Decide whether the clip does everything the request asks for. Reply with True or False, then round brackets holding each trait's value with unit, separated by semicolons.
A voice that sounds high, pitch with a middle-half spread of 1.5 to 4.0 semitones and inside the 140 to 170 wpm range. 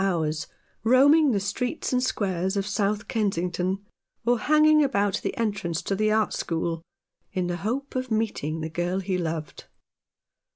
False (200 Hz; 5.1 semitones; 155 wpm)